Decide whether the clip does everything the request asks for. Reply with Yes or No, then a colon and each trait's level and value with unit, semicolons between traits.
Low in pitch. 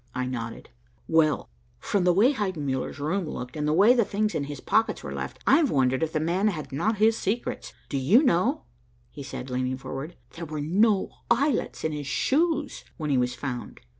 No: medium, 160 Hz